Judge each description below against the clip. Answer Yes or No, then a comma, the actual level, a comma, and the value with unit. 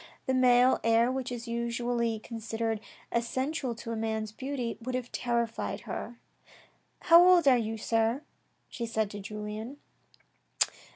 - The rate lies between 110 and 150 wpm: Yes, average, 140 wpm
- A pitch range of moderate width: No, narrow, 2.2 semitones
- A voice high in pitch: Yes, high, 235 Hz